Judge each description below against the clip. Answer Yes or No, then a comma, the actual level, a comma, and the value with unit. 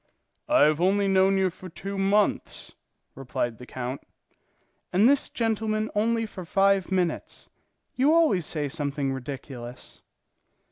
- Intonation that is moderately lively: No, wide, 6.6 semitones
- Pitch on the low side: No, high, 190 Hz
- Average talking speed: No, slow, 130 wpm